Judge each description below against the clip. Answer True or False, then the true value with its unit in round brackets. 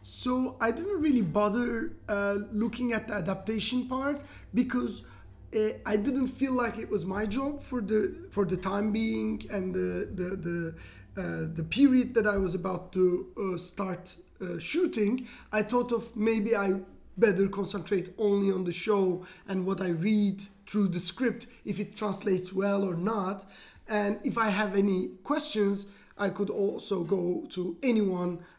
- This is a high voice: True (205 Hz)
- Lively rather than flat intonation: False (3.3 semitones)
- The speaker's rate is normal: True (165 wpm)